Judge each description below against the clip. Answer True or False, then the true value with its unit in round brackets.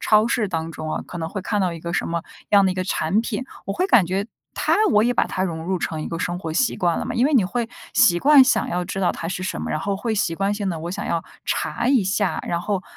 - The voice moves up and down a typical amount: True (3.9 semitones)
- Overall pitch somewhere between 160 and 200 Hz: True (190 Hz)